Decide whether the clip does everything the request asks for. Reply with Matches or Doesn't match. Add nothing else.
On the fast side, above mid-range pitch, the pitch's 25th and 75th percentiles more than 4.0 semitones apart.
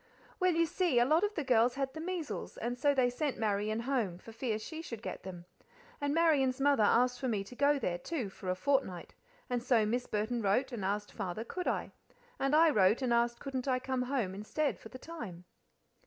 Matches